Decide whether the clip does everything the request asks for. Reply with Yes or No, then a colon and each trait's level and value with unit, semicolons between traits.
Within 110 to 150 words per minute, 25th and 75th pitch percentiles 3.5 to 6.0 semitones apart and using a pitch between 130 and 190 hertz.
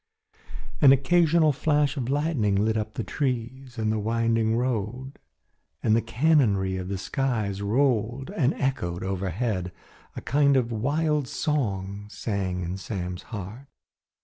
No: slow, 135 wpm; average, 5.3 semitones; low, 115 Hz